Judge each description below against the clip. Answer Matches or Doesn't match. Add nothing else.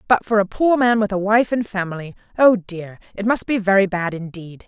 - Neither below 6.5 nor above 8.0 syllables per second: Doesn't match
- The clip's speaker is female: Matches